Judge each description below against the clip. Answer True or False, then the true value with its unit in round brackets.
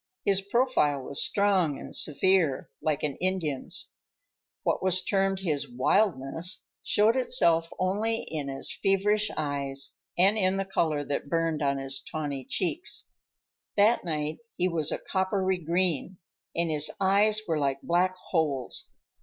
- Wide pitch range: False (4.7 semitones)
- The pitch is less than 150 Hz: False (175 Hz)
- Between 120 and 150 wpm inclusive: True (140 wpm)